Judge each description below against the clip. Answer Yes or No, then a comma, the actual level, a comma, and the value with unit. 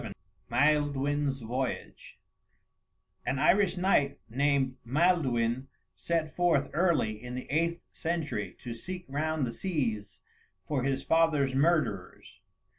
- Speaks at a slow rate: Yes, slow, 115 wpm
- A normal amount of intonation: Yes, average, 4.3 semitones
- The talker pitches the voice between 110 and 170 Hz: Yes, medium, 140 Hz